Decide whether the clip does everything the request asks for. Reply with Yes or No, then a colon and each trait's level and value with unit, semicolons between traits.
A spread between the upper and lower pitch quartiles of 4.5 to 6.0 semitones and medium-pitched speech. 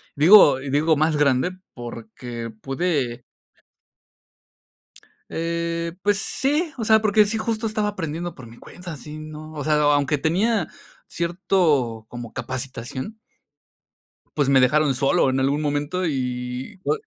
Yes: wide, 5.5 semitones; medium, 150 Hz